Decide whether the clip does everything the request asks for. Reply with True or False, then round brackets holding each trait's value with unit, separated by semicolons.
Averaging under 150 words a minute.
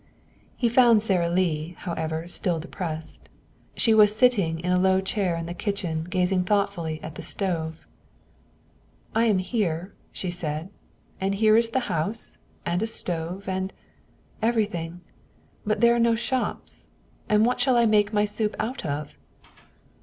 False (155 wpm)